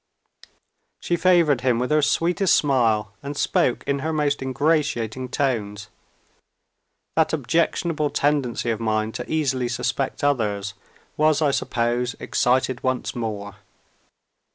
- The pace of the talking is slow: Yes, slow, 120 wpm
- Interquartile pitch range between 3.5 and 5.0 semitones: Yes, average, 4.4 semitones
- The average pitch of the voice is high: No, low, 130 Hz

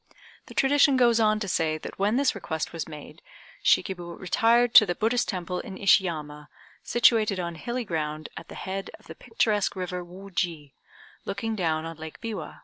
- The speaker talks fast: No, average, 175 wpm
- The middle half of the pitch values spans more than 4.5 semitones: Yes, average, 5.2 semitones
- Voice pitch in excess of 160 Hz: Yes, high, 190 Hz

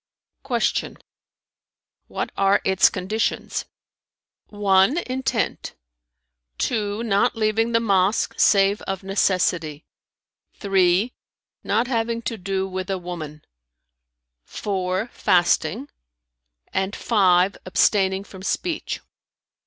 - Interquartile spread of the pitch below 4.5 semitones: Yes, average, 3.1 semitones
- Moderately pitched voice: No, high, 195 Hz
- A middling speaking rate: No, slow, 90 wpm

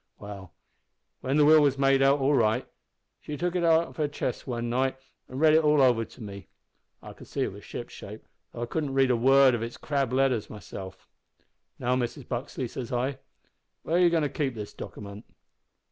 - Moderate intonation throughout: Yes, average, 3.6 semitones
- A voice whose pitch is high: No, low, 130 Hz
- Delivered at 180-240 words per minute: Yes, fast, 205 wpm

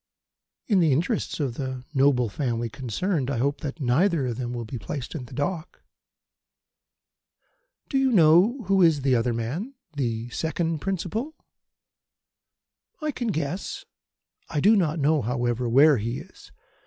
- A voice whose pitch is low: No, medium, 145 Hz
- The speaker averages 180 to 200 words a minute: No, average, 150 wpm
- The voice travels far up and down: Yes, wide, 6.3 semitones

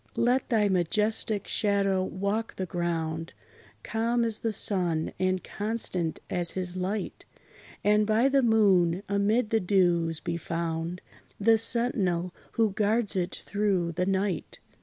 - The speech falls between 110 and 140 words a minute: Yes, slow, 135 wpm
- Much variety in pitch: No, average, 3.7 semitones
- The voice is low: No, high, 195 Hz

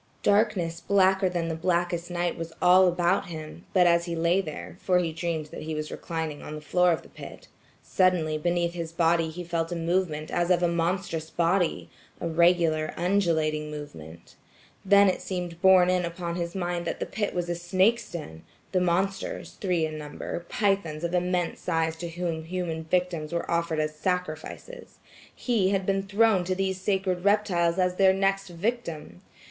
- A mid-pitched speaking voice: Yes, medium, 175 Hz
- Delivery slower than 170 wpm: No, average, 175 wpm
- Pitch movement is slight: Yes, narrow, 2.2 semitones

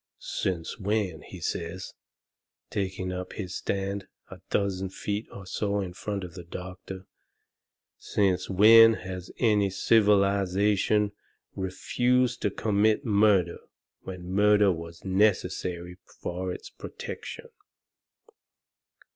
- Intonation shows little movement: Yes, narrow, 2.1 semitones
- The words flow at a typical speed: No, slow, 105 wpm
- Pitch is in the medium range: No, very low, 95 Hz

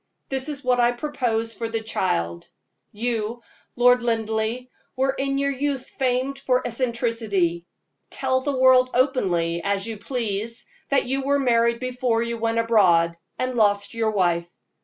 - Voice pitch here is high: Yes, high, 235 Hz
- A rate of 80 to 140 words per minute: No, average, 155 wpm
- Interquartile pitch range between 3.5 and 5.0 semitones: No, average, 2.9 semitones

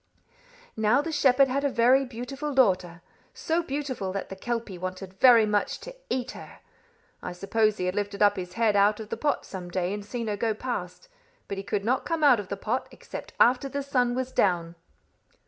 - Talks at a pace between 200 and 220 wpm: Yes, fast, 205 wpm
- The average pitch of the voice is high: Yes, high, 225 Hz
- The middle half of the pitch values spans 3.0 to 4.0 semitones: No, average, 4.8 semitones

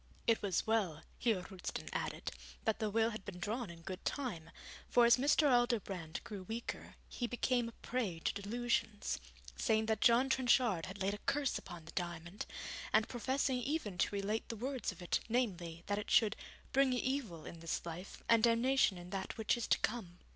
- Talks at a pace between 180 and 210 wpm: Yes, average, 190 wpm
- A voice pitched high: Yes, high, 220 Hz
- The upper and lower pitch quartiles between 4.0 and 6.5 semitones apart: Yes, average, 4.7 semitones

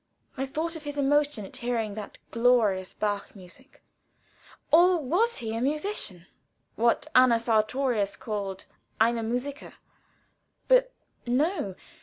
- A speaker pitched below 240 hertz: No, high, 245 Hz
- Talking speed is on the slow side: Yes, slow, 120 wpm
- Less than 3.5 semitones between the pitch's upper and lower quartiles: No, average, 5.3 semitones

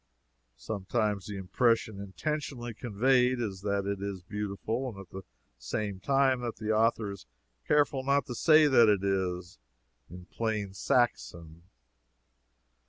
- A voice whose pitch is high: No, low, 105 Hz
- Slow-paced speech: Yes, slow, 130 wpm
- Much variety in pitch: No, average, 4.0 semitones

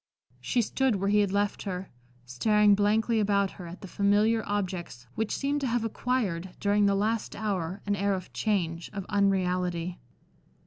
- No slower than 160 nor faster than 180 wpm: Yes, average, 170 wpm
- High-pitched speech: Yes, high, 200 Hz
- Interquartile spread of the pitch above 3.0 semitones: No, average, 2.7 semitones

